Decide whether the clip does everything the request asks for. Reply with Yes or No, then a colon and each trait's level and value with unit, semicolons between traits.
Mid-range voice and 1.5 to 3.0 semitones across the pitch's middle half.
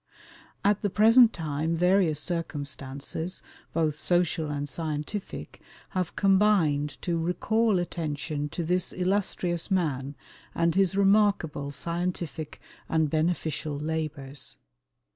No: medium, 165 Hz; average, 3.8 semitones